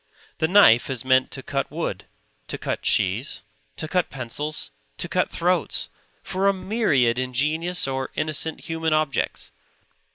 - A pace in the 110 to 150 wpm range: Yes, average, 140 wpm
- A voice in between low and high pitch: Yes, medium, 150 Hz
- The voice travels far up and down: No, average, 3.9 semitones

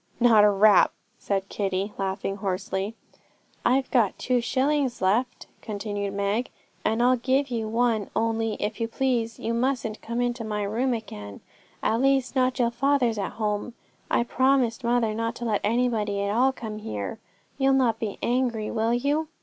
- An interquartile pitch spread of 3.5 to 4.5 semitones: No, average, 3.1 semitones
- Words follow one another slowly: No, average, 165 wpm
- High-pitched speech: Yes, high, 230 Hz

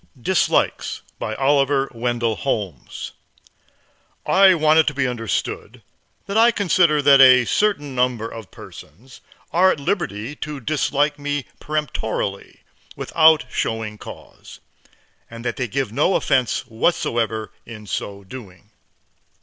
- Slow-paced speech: Yes, slow, 125 wpm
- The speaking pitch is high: No, low, 130 Hz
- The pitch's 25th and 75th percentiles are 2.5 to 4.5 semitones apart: No, average, 5.1 semitones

